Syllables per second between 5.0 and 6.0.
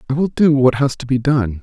Yes: 5.5 syllables/s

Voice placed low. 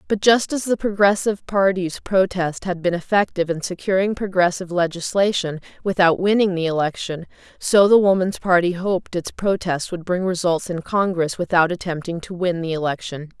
No: medium, 180 Hz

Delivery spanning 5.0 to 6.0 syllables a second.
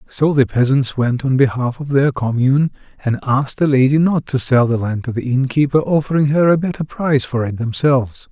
Yes: 5.5 syllables/s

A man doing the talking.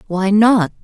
No: female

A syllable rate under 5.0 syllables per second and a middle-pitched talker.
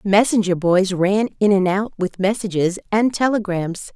No: 4.5 syllables/s; high, 200 Hz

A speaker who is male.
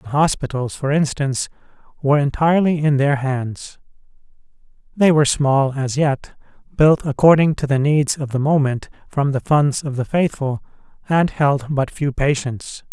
Yes: male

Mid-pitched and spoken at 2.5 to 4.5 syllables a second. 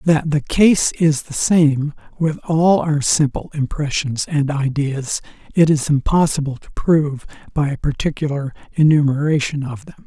Yes: medium, 150 Hz; 4.4 syllables/s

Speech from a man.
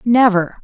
No: female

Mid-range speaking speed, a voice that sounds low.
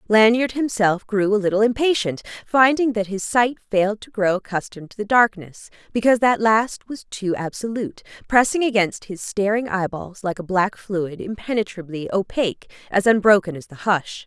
No: average, 165 wpm; high, 205 Hz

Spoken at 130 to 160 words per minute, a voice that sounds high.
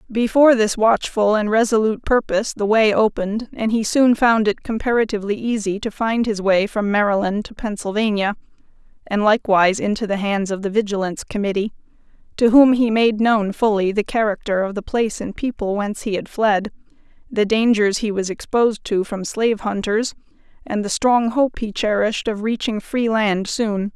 No: average, 175 wpm; high, 215 Hz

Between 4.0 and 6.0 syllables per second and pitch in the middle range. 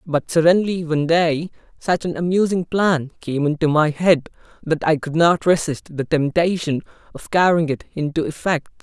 Yes: 4.8 syllables/s; medium, 160 Hz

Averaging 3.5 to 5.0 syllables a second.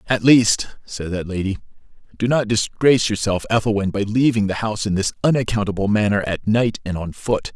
No: 5.6 syllables/s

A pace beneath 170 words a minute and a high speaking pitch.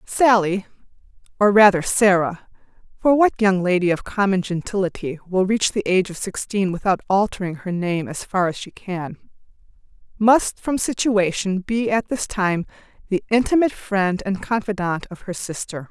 Yes: average, 155 wpm; high, 195 Hz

